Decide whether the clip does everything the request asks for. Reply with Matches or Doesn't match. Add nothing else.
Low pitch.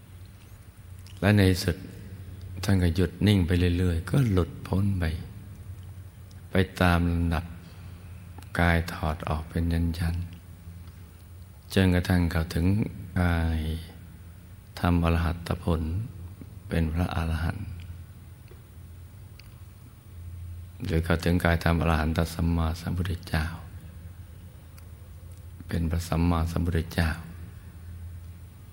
Matches